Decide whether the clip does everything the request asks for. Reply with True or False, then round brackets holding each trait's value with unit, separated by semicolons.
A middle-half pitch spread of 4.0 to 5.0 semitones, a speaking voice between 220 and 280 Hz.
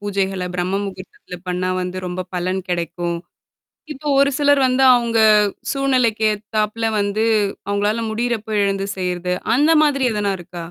False (4.3 semitones; 205 Hz)